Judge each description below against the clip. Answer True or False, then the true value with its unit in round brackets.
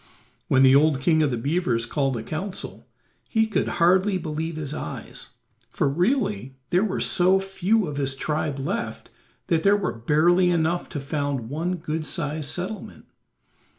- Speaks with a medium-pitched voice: True (160 Hz)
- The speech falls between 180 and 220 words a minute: False (160 wpm)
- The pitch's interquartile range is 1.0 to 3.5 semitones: False (4.5 semitones)